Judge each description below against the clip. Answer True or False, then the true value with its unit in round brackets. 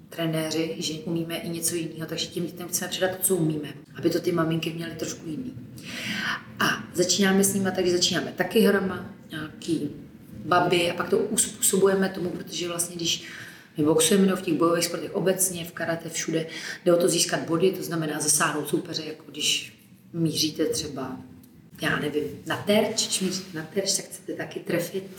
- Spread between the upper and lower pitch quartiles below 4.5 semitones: True (2.4 semitones)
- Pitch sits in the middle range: True (170 Hz)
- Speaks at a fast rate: True (175 wpm)